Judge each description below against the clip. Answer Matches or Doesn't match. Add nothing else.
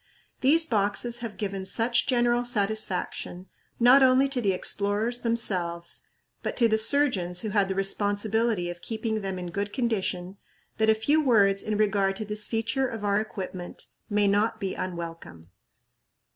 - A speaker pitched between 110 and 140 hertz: Doesn't match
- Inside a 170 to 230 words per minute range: Doesn't match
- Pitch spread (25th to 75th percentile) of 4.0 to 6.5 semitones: Doesn't match